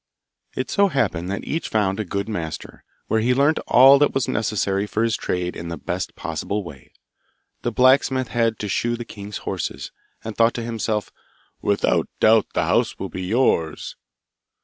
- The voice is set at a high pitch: No, low, 110 Hz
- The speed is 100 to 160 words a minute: No, average, 175 wpm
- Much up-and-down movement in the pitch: No, average, 3.6 semitones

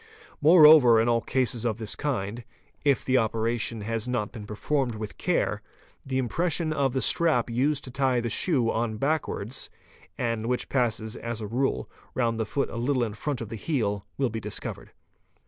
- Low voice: Yes, low, 120 Hz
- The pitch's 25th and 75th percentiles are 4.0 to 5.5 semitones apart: No, average, 3.3 semitones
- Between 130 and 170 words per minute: No, average, 180 wpm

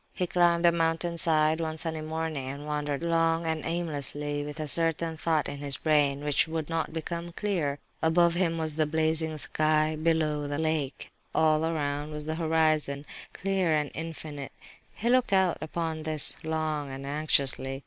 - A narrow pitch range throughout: Yes, narrow, 1.9 semitones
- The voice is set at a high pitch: No, medium, 155 Hz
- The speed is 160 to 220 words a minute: Yes, average, 170 wpm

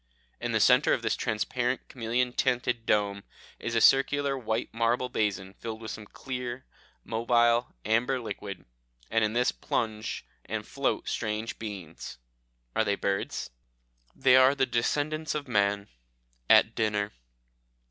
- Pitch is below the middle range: Yes, low, 115 Hz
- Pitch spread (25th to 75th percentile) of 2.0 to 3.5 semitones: Yes, average, 2.8 semitones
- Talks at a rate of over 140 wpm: No, slow, 135 wpm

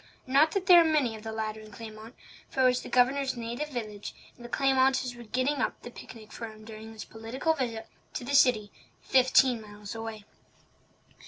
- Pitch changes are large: No, average, 3.2 semitones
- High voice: Yes, high, 240 Hz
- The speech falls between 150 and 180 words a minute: No, average, 195 wpm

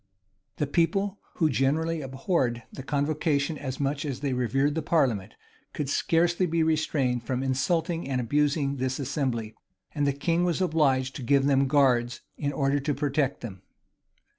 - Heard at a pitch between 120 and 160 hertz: Yes, medium, 140 Hz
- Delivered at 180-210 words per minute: No, average, 160 wpm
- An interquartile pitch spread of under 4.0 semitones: Yes, average, 3.1 semitones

